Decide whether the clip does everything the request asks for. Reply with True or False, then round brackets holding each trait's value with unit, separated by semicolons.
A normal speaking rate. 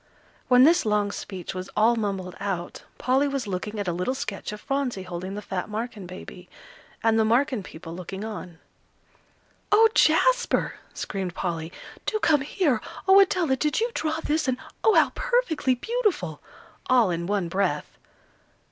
True (160 wpm)